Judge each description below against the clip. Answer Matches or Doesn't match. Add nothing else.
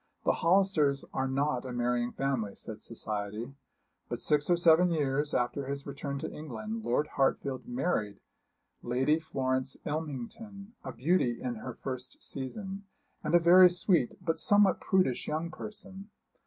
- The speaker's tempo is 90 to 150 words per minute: Matches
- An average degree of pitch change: Doesn't match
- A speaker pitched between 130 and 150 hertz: Matches